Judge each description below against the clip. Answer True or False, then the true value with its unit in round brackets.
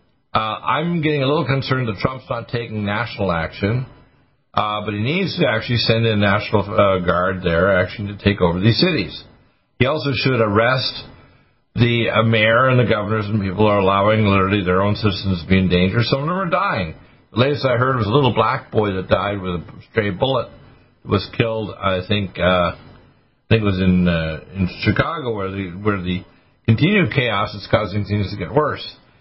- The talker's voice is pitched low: True (110 Hz)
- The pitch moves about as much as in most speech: True (4.3 semitones)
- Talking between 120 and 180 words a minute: False (205 wpm)